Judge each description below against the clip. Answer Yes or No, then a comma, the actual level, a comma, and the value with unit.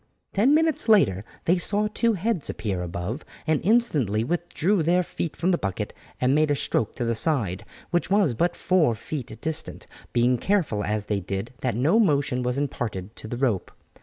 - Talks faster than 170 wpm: Yes, average, 185 wpm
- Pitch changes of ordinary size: No, wide, 8.3 semitones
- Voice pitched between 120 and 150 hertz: Yes, medium, 140 Hz